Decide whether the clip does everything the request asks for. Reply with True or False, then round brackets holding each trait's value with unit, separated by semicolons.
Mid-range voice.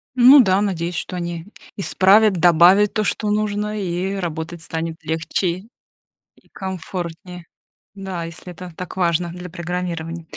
True (180 Hz)